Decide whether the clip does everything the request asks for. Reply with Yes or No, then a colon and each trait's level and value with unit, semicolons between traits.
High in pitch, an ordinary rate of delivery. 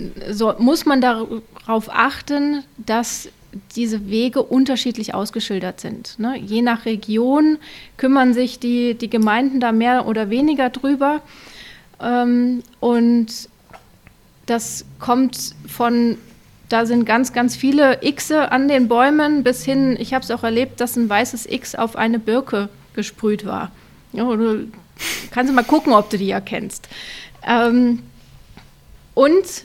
Yes: high, 240 Hz; average, 140 wpm